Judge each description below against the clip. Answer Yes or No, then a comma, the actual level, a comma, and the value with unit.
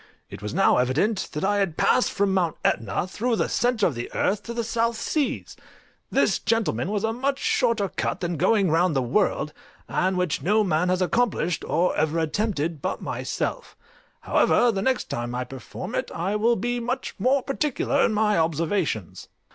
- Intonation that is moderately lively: No, wide, 6.1 semitones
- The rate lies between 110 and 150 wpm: No, average, 185 wpm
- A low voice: No, high, 195 Hz